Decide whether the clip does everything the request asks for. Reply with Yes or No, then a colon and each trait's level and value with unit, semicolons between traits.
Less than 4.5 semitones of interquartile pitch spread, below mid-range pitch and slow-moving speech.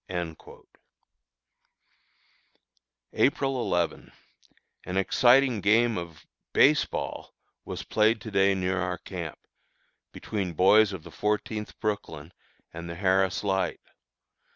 Yes: average, 3.2 semitones; very low, 95 Hz; slow, 105 wpm